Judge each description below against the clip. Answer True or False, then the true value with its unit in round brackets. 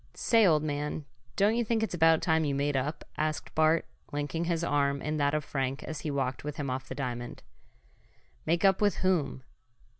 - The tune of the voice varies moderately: True (3.0 semitones)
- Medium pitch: True (150 Hz)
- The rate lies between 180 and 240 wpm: True (200 wpm)